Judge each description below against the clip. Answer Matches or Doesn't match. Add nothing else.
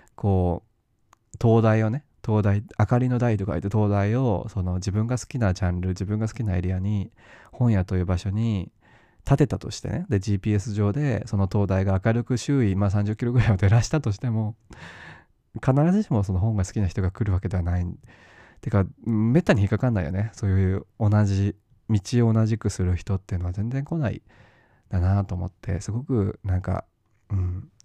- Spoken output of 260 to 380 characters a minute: Matches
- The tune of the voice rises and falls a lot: Doesn't match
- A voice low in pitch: Matches